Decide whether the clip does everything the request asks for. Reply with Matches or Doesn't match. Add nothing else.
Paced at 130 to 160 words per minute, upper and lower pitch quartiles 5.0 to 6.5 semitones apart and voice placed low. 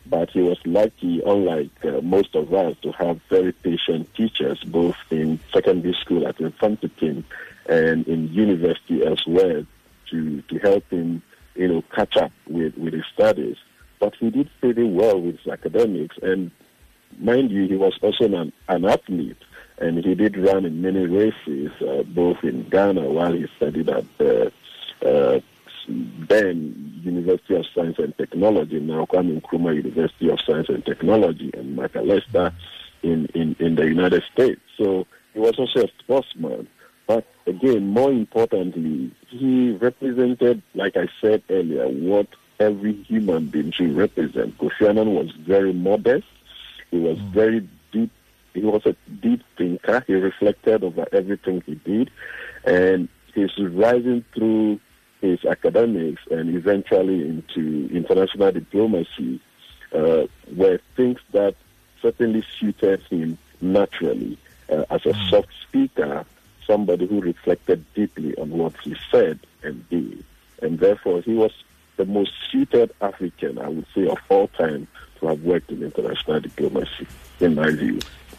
Matches